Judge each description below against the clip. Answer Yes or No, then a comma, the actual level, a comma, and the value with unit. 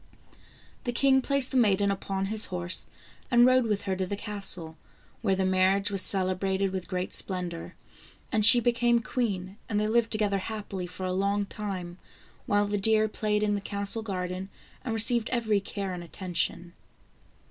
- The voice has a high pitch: Yes, high, 200 Hz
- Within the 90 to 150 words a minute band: No, average, 175 wpm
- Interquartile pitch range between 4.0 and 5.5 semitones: No, average, 2.7 semitones